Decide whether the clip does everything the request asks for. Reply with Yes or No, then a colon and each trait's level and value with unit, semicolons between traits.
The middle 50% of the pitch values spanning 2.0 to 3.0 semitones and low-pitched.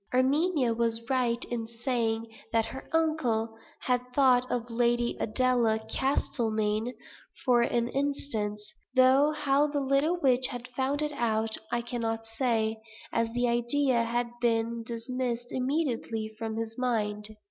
No: narrow, 2.5 semitones; high, 240 Hz